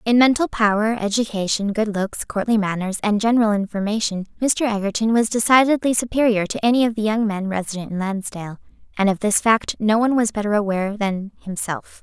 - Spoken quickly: No, average, 180 wpm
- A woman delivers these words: Yes, female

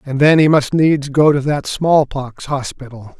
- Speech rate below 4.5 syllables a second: Yes, 4.2 syllables/s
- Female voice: No, male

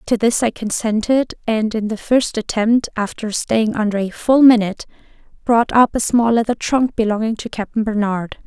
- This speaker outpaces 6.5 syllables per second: No, 4.9 syllables/s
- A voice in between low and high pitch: No, high, 225 Hz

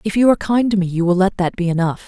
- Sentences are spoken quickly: Yes, fast, 345 wpm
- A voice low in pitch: No, high, 190 Hz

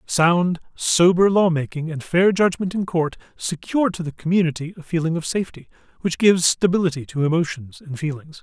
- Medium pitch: Yes, medium, 170 Hz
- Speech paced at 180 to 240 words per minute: No, average, 165 wpm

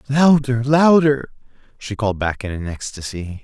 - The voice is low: Yes, low, 120 Hz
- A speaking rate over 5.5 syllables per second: No, 4.7 syllables/s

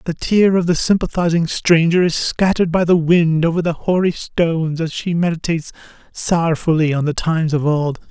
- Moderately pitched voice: Yes, medium, 165 Hz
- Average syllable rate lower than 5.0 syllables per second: No, 5.3 syllables/s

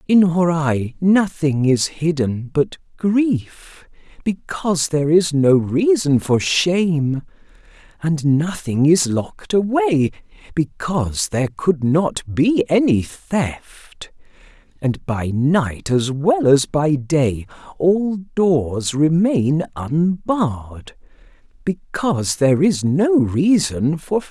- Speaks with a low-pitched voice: No, medium, 160 Hz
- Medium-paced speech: No, slow, 105 wpm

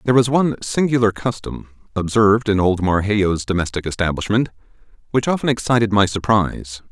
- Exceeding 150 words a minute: No, average, 140 wpm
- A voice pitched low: Yes, low, 105 Hz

